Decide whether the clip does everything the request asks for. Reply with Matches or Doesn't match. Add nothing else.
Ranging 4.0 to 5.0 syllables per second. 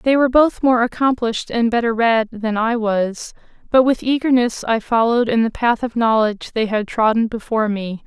Doesn't match